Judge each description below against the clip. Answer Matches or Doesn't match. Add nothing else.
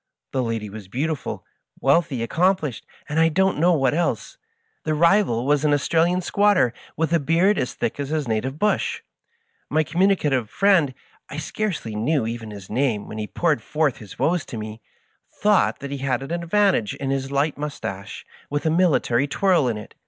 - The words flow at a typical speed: Matches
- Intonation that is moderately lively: Doesn't match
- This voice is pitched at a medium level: Matches